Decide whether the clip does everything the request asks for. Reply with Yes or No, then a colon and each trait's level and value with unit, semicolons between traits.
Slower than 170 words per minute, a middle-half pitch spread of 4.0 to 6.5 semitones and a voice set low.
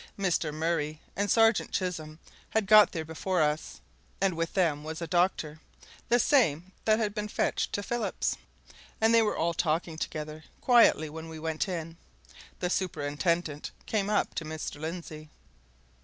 No: average, 155 wpm; average, 4.3 semitones; medium, 170 Hz